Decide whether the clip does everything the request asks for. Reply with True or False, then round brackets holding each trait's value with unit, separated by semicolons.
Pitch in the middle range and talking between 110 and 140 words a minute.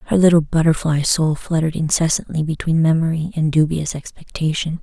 True (160 Hz; 135 wpm)